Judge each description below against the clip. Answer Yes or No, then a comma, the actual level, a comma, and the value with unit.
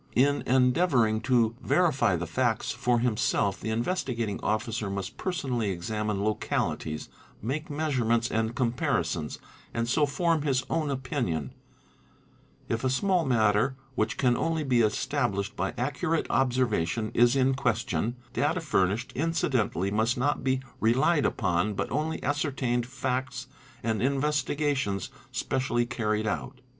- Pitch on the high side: No, low, 120 Hz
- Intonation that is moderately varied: Yes, average, 4.1 semitones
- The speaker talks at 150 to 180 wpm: No, average, 140 wpm